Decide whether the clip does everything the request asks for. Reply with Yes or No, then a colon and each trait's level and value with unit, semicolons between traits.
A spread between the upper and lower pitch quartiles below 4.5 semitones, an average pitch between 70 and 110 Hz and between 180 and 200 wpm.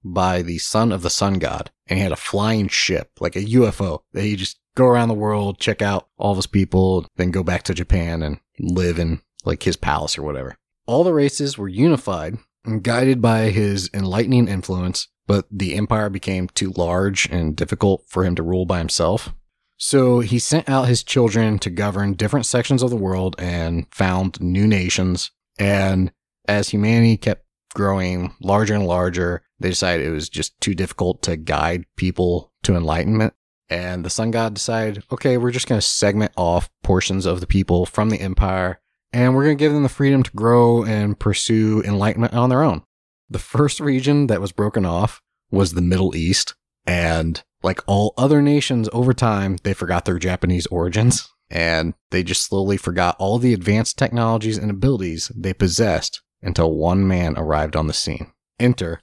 Yes: average, 4.0 semitones; low, 100 Hz; average, 185 wpm